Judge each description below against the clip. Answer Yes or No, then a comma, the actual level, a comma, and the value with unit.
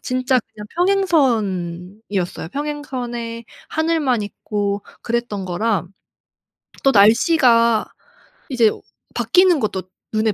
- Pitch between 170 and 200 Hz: No, high, 230 Hz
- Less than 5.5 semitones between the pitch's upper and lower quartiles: Yes, average, 5.1 semitones